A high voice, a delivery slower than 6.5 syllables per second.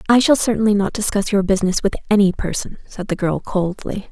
Yes: high, 200 Hz; 5.9 syllables/s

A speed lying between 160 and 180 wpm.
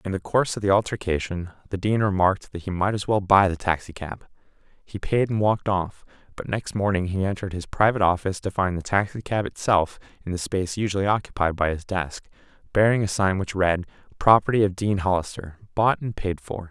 No: average, 200 wpm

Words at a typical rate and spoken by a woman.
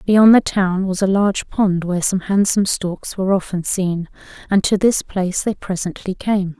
Yes: average, 190 wpm; female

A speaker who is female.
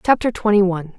Yes: female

